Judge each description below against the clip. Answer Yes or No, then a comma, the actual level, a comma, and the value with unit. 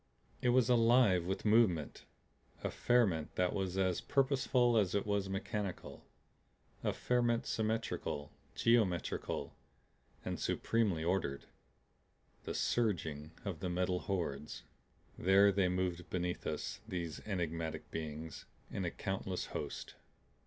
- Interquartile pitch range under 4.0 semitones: No, average, 4.4 semitones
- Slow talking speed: Yes, slow, 115 wpm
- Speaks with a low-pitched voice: Yes, very low, 95 Hz